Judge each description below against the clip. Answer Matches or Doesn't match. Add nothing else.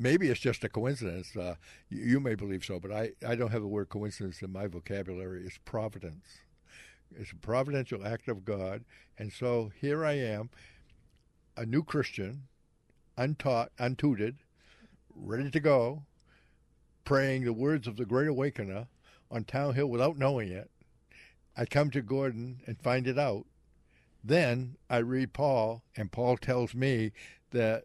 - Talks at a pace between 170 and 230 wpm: Doesn't match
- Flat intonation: Doesn't match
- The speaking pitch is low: Matches